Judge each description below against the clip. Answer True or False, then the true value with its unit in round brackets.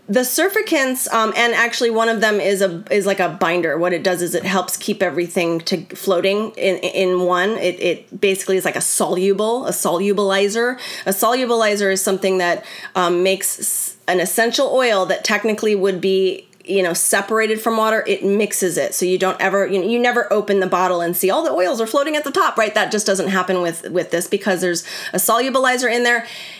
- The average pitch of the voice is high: True (195 Hz)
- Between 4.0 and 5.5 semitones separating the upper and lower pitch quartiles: False (3.3 semitones)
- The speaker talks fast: True (210 wpm)